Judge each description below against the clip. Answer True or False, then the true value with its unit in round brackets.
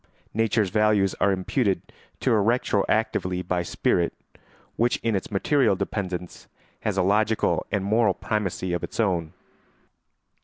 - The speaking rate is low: True (130 wpm)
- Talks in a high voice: False (100 Hz)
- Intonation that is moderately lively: True (3.1 semitones)